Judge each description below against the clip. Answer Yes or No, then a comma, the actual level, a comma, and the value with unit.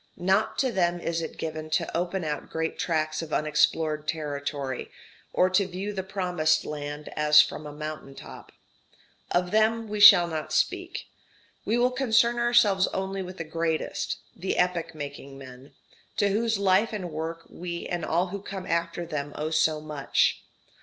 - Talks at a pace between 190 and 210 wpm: No, average, 165 wpm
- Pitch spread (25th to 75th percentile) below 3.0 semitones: No, average, 3.8 semitones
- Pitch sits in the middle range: Yes, medium, 170 Hz